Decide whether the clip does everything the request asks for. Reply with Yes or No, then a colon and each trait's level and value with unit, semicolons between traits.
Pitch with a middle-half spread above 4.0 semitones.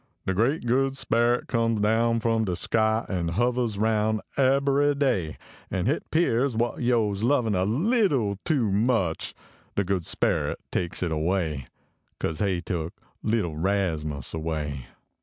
Yes: wide, 5.4 semitones